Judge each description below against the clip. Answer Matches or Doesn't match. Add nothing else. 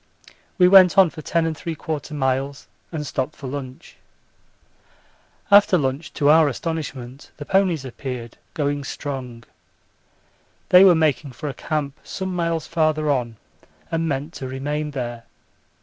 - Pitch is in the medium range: Matches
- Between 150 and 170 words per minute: Doesn't match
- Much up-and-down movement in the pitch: Doesn't match